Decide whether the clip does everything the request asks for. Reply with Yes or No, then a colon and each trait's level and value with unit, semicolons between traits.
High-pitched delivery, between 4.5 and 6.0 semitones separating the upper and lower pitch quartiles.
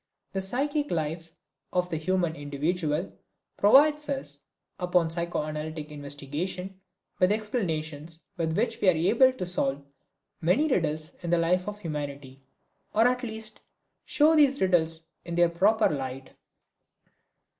No: medium, 175 Hz; average, 5.2 semitones